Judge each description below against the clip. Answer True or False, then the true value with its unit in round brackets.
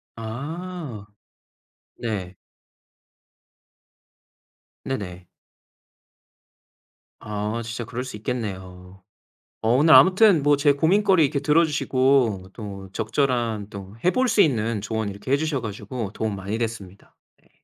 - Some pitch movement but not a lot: False (5.8 semitones)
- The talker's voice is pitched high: False (115 Hz)